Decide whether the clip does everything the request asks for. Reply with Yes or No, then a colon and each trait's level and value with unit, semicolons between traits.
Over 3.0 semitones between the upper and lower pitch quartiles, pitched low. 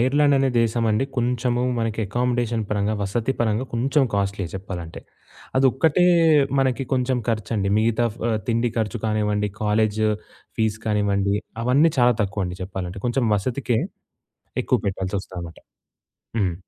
Yes: average, 3.5 semitones; low, 110 Hz